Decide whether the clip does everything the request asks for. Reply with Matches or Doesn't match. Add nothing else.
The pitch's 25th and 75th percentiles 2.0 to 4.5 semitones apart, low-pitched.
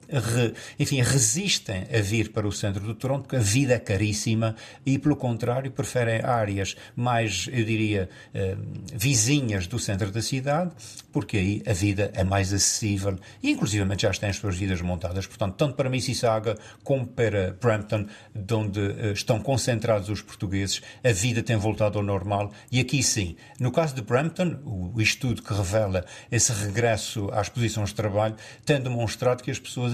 Matches